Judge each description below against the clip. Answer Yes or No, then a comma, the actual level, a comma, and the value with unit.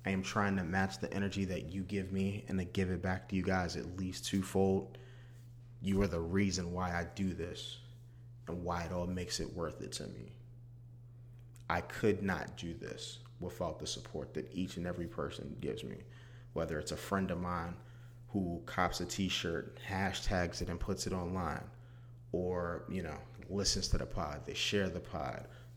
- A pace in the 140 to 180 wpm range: No, average, 190 wpm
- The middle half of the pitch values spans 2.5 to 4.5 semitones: No, average, 5.1 semitones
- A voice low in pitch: Yes, very low, 95 Hz